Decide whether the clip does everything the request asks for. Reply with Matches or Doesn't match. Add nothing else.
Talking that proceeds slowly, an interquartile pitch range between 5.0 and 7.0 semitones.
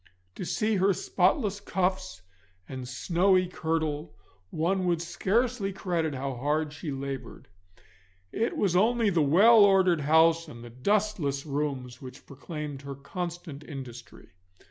Matches